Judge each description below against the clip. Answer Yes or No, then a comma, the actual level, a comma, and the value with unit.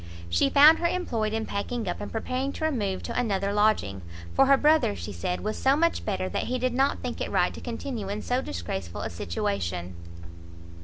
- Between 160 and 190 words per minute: No, fast, 205 wpm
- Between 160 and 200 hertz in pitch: No, high, 215 Hz